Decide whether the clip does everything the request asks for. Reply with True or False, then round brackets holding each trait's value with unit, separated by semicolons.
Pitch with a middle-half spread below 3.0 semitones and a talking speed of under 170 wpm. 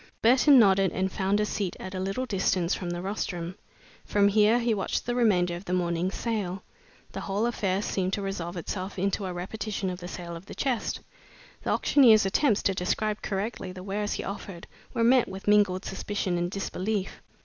False (2.5 semitones; 195 wpm)